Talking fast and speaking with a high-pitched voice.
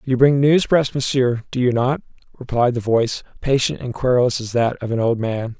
No: fast, 215 wpm; low, 125 Hz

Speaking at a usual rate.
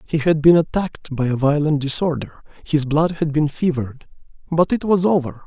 Yes: average, 185 wpm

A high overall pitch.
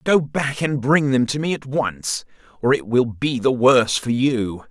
No: low, 130 Hz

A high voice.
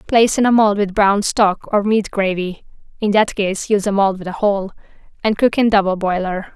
Yes: high, 200 Hz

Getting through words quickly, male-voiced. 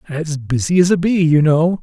Yes: fast, 230 wpm; male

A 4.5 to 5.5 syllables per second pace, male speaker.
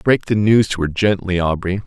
Yes: 5.2 syllables/s; male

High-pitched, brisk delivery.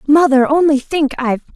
No: very high, 285 Hz; average, 155 wpm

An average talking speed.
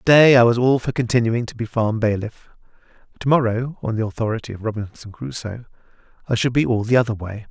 No: fast, 210 wpm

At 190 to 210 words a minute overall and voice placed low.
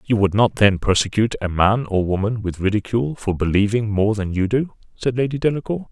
Yes: fast, 205 wpm; low, 110 Hz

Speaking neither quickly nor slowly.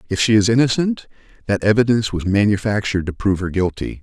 Yes: average, 180 wpm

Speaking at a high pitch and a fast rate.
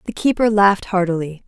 No: high, 195 Hz; average, 165 wpm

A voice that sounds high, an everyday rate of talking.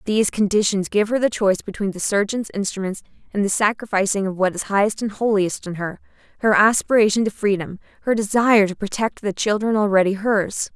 Yes: high, 205 Hz; average, 180 wpm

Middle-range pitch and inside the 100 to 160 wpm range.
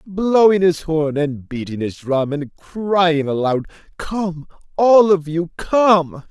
Yes: medium, 165 Hz; average, 145 wpm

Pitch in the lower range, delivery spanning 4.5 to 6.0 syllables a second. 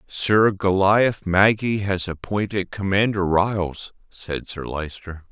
No: very low, 95 Hz; 3.6 syllables/s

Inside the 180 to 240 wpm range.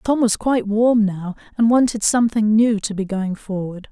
Yes: average, 200 wpm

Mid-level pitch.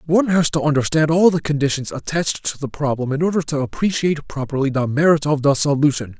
Yes: medium, 150 Hz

